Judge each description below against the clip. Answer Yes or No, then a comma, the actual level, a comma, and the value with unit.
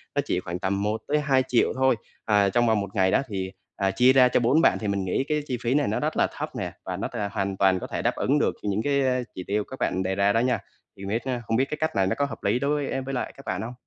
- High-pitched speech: No, low, 115 Hz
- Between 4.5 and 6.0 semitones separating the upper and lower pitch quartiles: Yes, average, 5.1 semitones